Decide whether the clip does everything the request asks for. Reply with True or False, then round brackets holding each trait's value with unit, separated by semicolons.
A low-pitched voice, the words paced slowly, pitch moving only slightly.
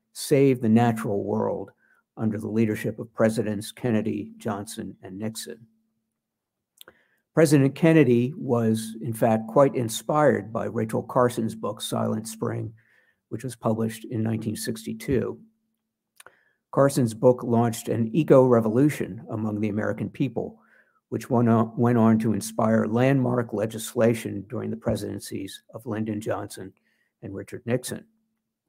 True (115 Hz; 125 wpm; 2.0 semitones)